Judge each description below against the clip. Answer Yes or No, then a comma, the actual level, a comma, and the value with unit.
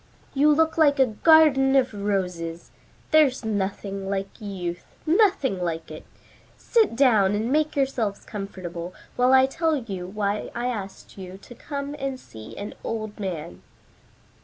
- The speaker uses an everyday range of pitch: No, wide, 6.0 semitones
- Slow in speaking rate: No, average, 145 wpm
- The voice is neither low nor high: No, high, 215 Hz